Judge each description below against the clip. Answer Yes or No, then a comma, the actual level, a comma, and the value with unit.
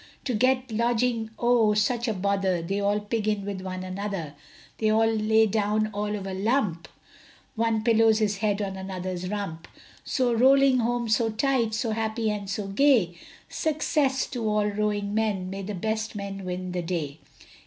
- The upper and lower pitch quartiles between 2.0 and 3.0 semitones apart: Yes, narrow, 2.6 semitones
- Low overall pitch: No, high, 210 Hz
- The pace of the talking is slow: No, average, 175 wpm